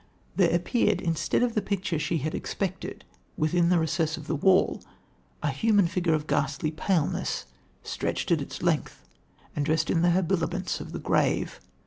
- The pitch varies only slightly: No, average, 3.1 semitones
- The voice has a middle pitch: Yes, medium, 170 Hz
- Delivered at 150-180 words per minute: Yes, average, 165 wpm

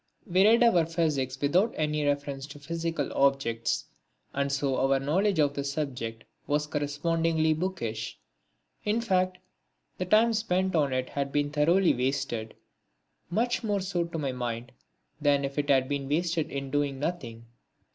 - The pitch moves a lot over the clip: No, average, 4.0 semitones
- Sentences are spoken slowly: No, average, 155 wpm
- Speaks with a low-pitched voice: No, medium, 145 Hz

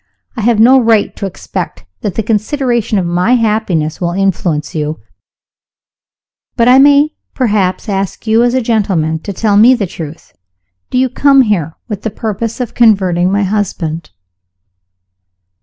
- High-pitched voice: Yes, high, 210 Hz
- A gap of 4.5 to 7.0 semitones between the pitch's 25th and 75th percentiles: Yes, average, 4.8 semitones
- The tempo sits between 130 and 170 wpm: Yes, average, 155 wpm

